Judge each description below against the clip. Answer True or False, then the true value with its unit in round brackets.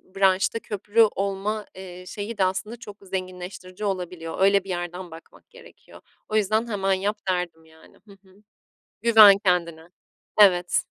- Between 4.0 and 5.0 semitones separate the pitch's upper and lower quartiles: False (2.4 semitones)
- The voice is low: False (190 Hz)